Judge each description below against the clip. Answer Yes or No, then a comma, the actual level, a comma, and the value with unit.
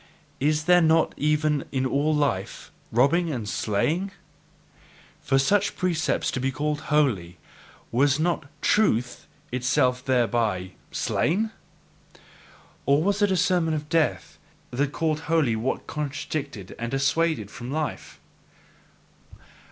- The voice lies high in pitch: No, medium, 145 Hz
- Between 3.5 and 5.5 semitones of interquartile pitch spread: Yes, average, 4.1 semitones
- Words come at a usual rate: No, slow, 120 wpm